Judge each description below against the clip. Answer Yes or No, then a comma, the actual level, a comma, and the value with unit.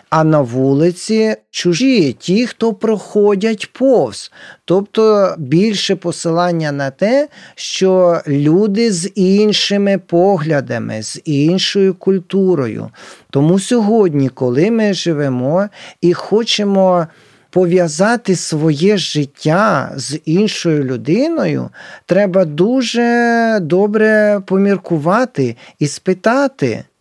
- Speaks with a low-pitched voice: No, medium, 185 Hz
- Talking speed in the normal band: No, slow, 90 wpm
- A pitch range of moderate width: Yes, average, 4.7 semitones